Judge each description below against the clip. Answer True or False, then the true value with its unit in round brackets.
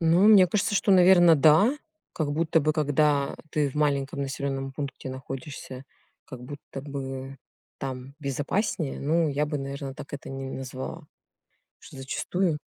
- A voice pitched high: False (145 Hz)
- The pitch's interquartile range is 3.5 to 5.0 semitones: False (3.0 semitones)